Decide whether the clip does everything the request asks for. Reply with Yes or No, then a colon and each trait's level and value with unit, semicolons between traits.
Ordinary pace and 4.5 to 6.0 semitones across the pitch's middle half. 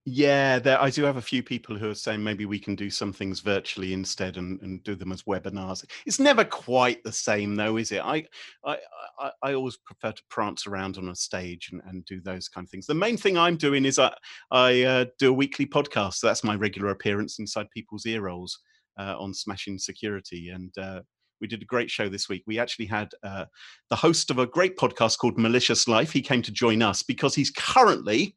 No: fast, 225 wpm; average, 4.8 semitones